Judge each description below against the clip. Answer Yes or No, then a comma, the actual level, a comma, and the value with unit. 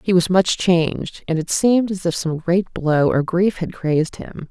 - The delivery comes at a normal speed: No, fast, 225 wpm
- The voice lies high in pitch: No, medium, 175 Hz